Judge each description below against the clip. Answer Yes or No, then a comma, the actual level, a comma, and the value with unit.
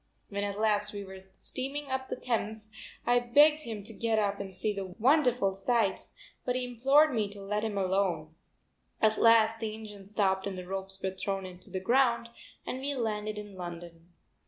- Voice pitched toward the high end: Yes, high, 210 Hz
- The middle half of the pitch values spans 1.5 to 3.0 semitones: No, average, 3.6 semitones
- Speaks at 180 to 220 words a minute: Yes, average, 190 wpm